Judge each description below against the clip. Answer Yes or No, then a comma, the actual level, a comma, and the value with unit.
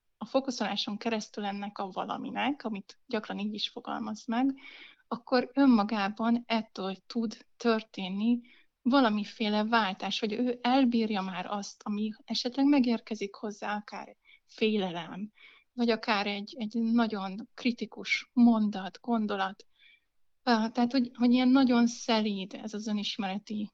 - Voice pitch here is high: Yes, high, 225 Hz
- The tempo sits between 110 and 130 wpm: Yes, average, 120 wpm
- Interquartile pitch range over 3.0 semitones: No, average, 2.7 semitones